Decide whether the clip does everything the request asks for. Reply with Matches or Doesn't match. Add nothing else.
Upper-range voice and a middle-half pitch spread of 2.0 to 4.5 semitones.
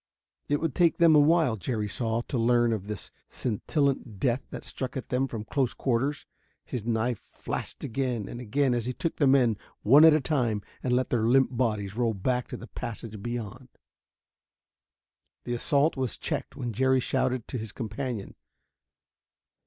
Doesn't match